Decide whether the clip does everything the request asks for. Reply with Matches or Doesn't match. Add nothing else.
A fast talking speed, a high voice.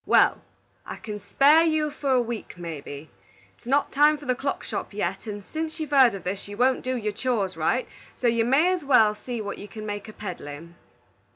Matches